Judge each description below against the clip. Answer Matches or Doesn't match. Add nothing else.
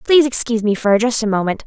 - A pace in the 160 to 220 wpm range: Doesn't match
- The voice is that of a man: Doesn't match